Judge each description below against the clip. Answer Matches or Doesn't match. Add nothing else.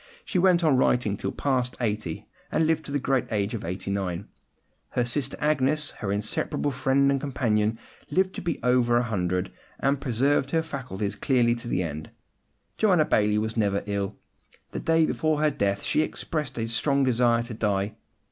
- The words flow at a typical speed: Matches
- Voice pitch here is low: Matches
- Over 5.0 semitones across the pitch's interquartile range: Matches